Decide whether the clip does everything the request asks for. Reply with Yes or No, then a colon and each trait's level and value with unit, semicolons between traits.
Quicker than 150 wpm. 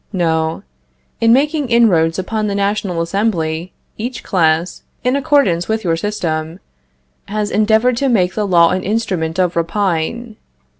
No: average, 140 wpm